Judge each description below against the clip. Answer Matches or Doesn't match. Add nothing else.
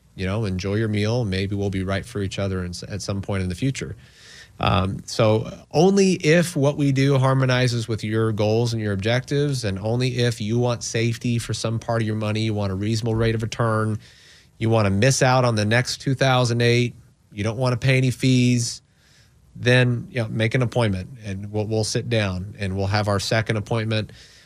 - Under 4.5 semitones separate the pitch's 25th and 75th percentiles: Matches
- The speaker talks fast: Matches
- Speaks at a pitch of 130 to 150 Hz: Doesn't match